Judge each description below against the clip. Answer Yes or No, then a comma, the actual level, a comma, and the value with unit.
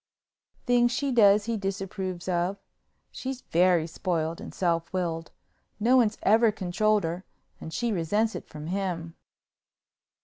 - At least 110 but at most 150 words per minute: Yes, slow, 135 wpm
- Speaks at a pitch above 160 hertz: Yes, high, 190 Hz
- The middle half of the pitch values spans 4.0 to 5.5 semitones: Yes, average, 4.3 semitones